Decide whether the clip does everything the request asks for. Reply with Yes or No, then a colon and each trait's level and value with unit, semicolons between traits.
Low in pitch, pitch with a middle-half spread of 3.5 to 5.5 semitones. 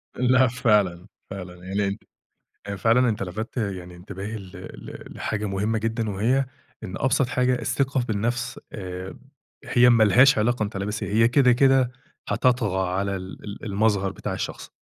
Yes: low, 110 Hz; average, 3.9 semitones